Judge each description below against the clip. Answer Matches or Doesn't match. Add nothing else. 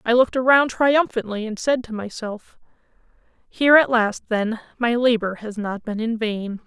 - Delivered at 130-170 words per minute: Matches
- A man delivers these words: Doesn't match